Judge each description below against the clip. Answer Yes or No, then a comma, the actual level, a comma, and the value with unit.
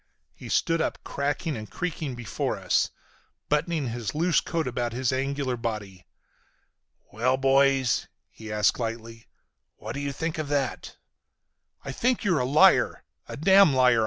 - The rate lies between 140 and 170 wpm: Yes, average, 150 wpm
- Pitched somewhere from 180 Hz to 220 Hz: No, low, 135 Hz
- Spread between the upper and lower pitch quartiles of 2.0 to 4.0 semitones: No, average, 4.5 semitones